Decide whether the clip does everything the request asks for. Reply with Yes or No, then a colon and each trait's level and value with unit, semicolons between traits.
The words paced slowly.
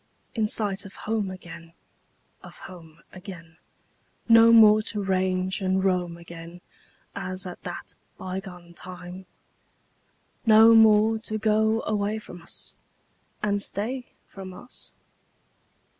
Yes: slow, 115 wpm